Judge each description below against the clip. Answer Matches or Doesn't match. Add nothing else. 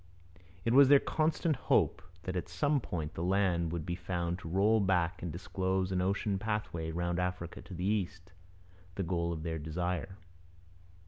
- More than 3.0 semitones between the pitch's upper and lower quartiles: Doesn't match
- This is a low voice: Matches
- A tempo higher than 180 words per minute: Doesn't match